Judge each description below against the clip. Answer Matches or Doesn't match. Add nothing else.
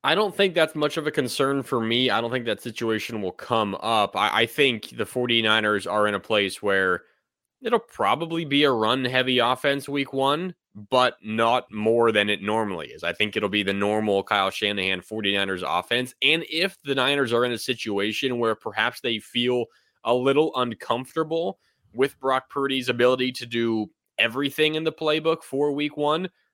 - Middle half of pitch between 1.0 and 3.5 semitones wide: Doesn't match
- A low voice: Matches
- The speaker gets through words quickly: Doesn't match